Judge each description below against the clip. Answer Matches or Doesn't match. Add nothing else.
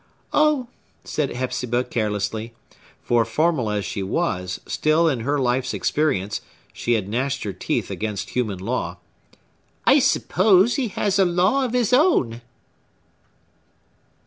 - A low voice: Matches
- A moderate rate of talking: Doesn't match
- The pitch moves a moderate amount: Doesn't match